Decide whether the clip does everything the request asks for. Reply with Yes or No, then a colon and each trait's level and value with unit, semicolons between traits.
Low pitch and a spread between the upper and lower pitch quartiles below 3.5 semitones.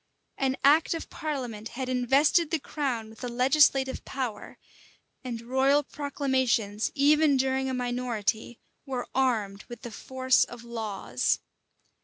No: very high, 255 Hz; average, 2.8 semitones